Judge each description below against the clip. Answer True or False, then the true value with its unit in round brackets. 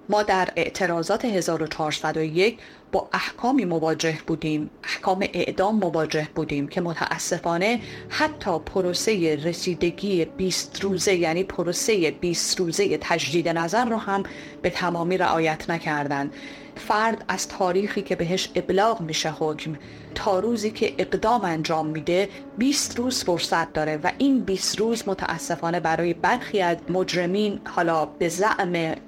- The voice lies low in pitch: False (175 Hz)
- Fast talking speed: False (125 wpm)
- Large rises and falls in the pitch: False (3.4 semitones)